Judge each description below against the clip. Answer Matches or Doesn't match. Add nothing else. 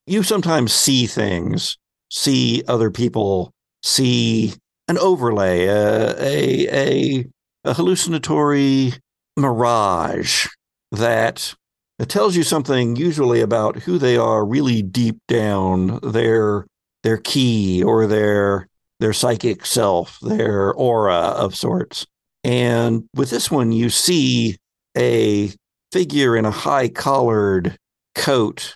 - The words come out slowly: Matches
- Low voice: Matches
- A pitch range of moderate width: Matches